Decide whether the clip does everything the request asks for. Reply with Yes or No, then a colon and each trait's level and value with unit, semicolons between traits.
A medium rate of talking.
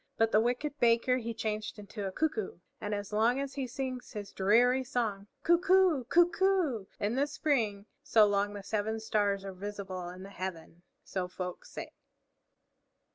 Yes: average, 175 wpm